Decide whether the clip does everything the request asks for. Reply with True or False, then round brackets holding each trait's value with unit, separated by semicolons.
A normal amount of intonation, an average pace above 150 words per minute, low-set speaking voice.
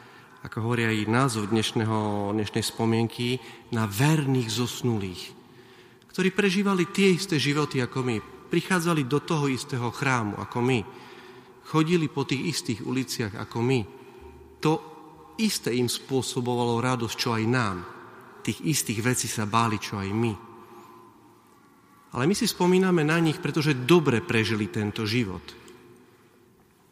False (4.7 semitones; 125 wpm; 125 Hz)